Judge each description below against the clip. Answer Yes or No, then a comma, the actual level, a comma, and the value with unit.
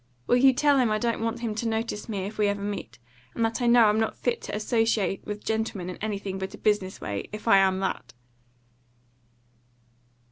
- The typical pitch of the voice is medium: No, high, 215 Hz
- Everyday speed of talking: No, fast, 210 wpm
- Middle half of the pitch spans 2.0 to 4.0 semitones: Yes, narrow, 2.4 semitones